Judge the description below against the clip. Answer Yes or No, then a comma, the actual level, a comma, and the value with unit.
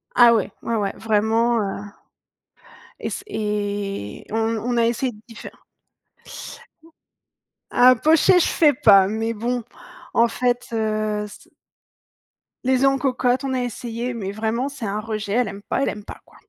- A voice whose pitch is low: No, high, 230 Hz